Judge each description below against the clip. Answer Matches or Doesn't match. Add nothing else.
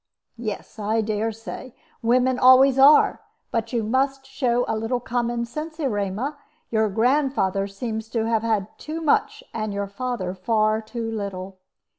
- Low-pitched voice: Doesn't match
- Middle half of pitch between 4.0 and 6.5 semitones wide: Doesn't match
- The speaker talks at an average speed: Matches